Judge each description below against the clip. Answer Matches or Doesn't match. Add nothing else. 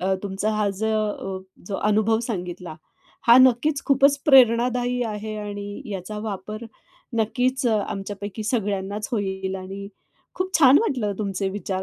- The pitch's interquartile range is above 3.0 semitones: Matches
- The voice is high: Matches